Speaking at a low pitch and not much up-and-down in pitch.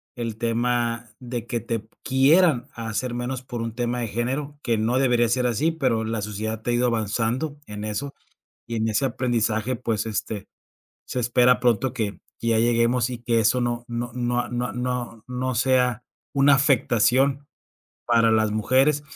Yes: low, 120 Hz; narrow, 2.0 semitones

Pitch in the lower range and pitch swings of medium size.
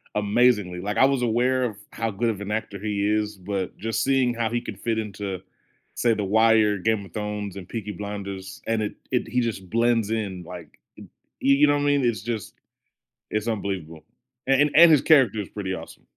Yes: low, 110 Hz; average, 3.0 semitones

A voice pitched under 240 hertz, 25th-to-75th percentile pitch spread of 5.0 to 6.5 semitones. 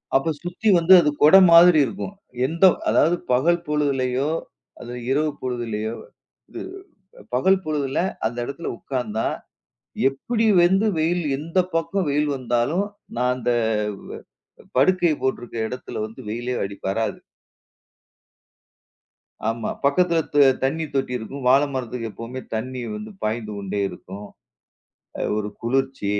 Yes: low, 135 Hz; wide, 5.6 semitones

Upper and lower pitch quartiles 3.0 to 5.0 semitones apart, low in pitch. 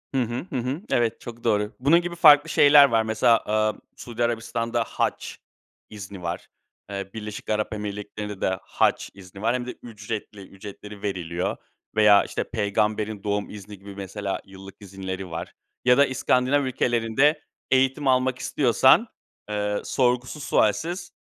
Yes: average, 3.8 semitones; low, 110 Hz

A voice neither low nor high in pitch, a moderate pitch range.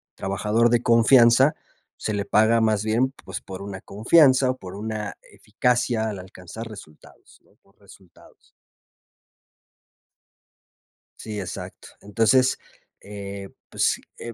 No: low, 110 Hz; average, 3.0 semitones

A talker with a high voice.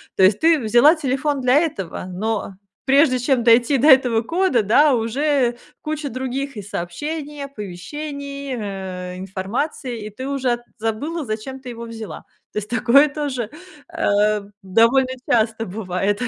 Yes: high, 245 Hz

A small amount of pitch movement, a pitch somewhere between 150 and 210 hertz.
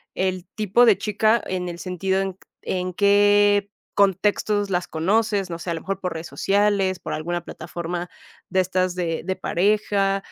Yes: narrow, 2.3 semitones; high, 190 Hz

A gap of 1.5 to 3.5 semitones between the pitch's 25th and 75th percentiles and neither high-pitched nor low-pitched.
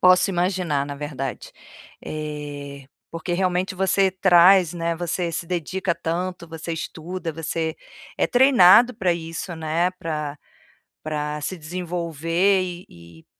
Yes: average, 3.0 semitones; medium, 170 Hz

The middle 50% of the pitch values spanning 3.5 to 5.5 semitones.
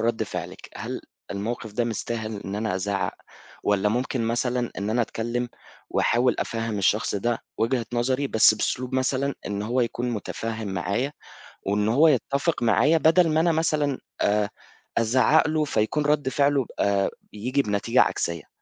Yes: average, 4.1 semitones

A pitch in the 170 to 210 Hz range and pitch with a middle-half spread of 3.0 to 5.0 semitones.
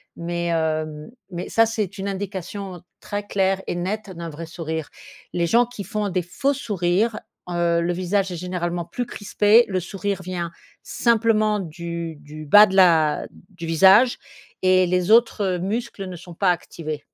Yes: medium, 185 Hz; average, 3.3 semitones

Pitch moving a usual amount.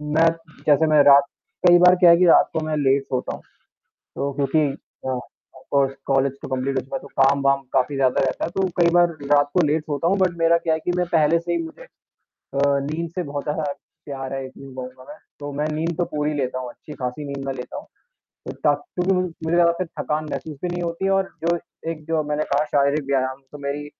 Yes: average, 3.5 semitones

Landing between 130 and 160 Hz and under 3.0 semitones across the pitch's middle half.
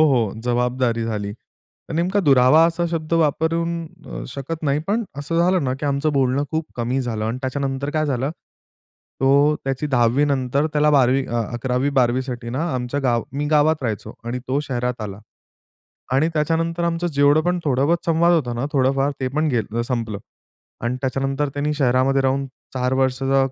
No: low, 135 Hz; average, 3.3 semitones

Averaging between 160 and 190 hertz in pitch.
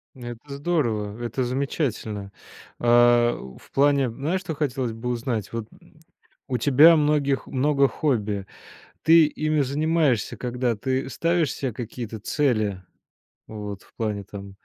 No: low, 125 Hz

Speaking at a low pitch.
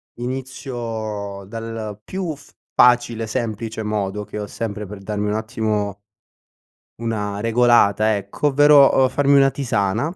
Yes: low, 110 Hz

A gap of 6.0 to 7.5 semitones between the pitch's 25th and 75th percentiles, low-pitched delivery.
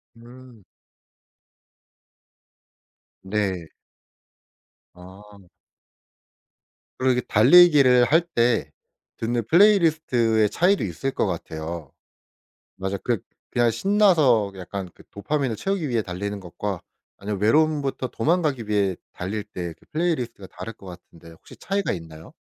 Yes: wide, 7.1 semitones; low, 115 Hz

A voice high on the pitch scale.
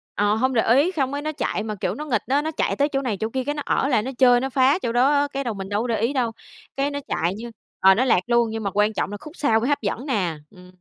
Yes: high, 245 Hz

